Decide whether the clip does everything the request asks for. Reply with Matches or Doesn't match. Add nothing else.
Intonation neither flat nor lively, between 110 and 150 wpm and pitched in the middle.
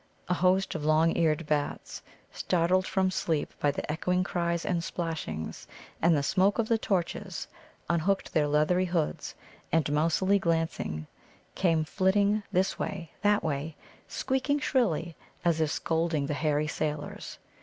Matches